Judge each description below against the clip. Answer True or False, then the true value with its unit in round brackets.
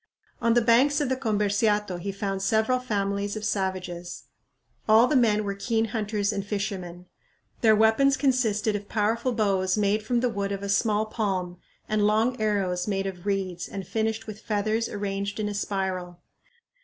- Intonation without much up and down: True (2.1 semitones)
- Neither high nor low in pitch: False (210 Hz)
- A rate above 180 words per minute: False (170 wpm)